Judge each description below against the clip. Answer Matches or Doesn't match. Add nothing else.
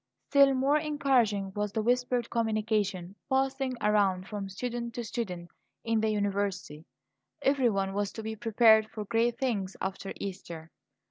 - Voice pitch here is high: Matches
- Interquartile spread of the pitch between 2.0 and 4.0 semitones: Matches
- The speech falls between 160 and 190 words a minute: Doesn't match